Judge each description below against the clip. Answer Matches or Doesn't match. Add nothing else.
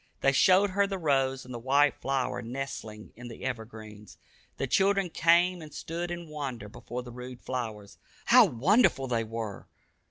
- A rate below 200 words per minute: Matches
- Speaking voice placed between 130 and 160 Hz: Matches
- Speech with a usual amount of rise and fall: Doesn't match